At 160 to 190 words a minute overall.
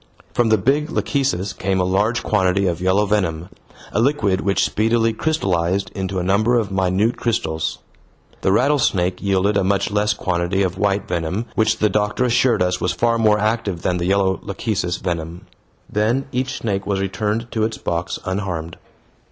Yes: average, 170 wpm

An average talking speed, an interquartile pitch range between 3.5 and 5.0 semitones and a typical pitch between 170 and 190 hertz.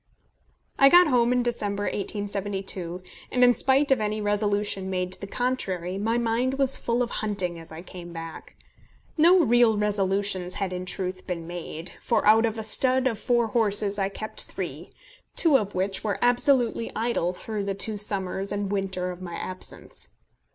No: average, 175 wpm; average, 4.1 semitones; high, 205 Hz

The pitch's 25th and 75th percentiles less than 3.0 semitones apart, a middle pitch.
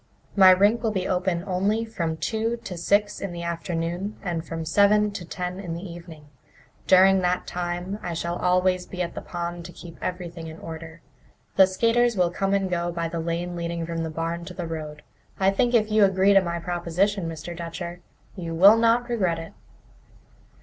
Yes: narrow, 2.6 semitones; medium, 180 Hz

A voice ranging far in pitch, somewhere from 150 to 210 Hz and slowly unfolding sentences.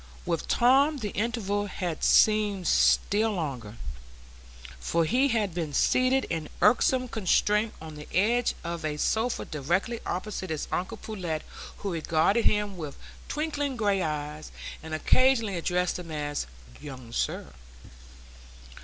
Yes: wide, 6.1 semitones; high, 190 Hz; slow, 130 wpm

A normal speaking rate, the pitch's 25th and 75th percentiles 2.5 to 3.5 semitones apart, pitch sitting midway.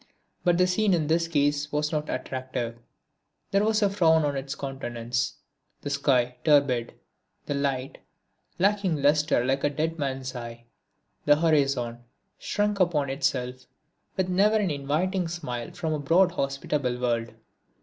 No: average, 145 wpm; average, 4.6 semitones; medium, 145 Hz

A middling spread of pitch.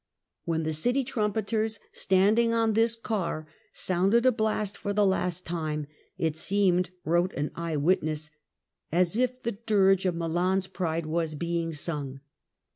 Yes: average, 4.7 semitones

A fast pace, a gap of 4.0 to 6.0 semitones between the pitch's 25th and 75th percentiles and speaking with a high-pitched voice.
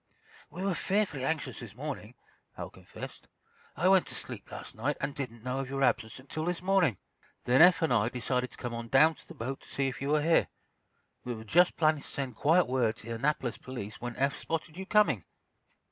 No: fast, 220 wpm; average, 4.9 semitones; low, 135 Hz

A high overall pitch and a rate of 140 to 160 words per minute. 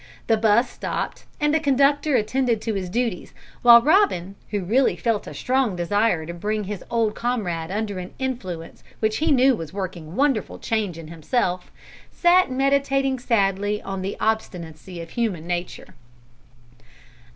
Yes: high, 215 Hz; average, 155 wpm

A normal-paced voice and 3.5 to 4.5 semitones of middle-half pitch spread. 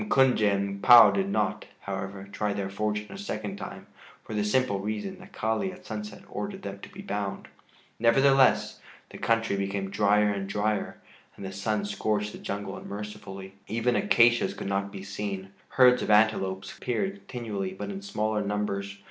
No: average, 170 wpm; average, 2.8 semitones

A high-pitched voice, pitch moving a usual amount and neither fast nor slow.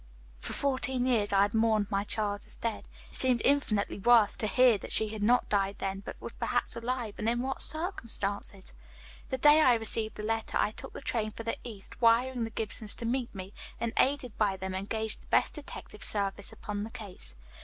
No: high, 220 Hz; average, 3.1 semitones; fast, 210 wpm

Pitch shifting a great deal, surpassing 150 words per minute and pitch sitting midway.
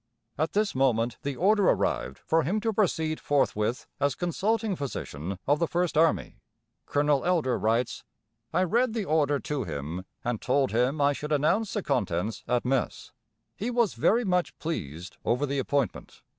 Yes: wide, 6.6 semitones; average, 165 wpm; medium, 145 Hz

